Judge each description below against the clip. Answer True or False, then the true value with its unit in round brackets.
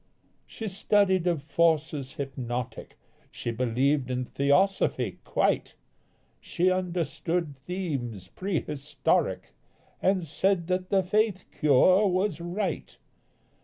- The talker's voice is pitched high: False (170 Hz)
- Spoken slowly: True (95 wpm)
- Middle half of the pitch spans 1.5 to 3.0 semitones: False (5.5 semitones)